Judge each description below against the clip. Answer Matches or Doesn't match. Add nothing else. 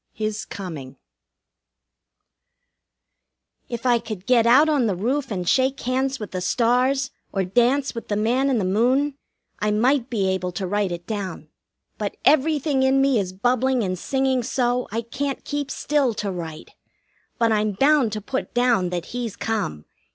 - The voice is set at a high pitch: Matches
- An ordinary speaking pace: Matches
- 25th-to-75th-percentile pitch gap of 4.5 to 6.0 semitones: Matches